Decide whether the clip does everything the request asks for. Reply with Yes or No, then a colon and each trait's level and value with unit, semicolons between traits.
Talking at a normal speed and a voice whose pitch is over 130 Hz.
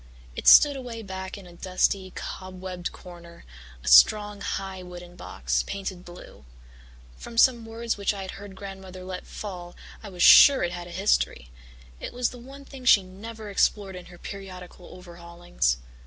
Yes: average, 170 wpm; high, 190 Hz